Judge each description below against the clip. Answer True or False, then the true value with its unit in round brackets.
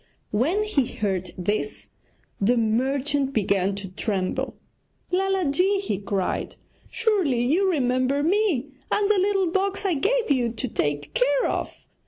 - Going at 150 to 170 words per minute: False (140 wpm)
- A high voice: True (275 Hz)